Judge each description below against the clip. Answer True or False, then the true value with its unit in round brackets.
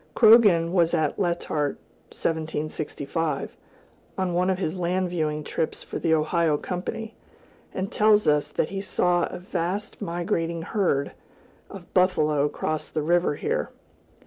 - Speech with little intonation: False (3.2 semitones)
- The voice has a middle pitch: True (170 Hz)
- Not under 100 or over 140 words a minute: True (135 wpm)